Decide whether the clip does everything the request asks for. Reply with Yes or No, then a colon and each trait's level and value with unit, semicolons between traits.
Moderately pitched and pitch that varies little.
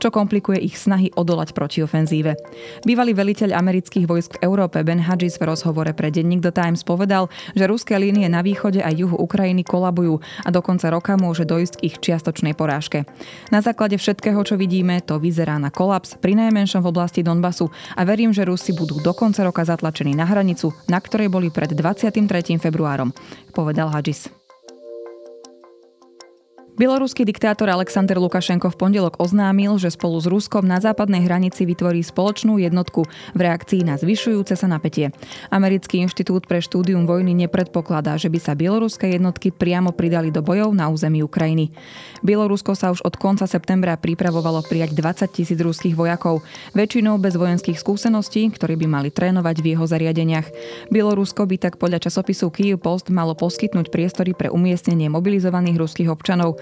No: medium, 180 Hz; average, 3.0 semitones